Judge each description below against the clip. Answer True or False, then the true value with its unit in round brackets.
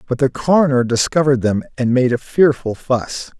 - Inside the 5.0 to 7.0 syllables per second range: True (5.3 syllables/s)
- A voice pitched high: False (130 Hz)